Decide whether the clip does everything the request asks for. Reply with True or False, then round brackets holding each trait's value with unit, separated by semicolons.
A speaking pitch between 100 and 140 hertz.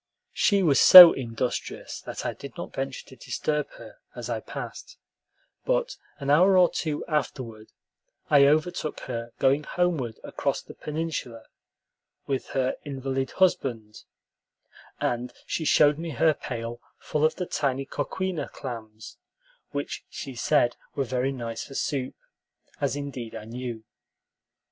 True (135 Hz)